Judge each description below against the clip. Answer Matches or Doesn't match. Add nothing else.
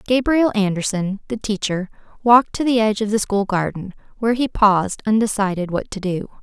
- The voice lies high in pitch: Matches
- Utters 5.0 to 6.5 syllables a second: Matches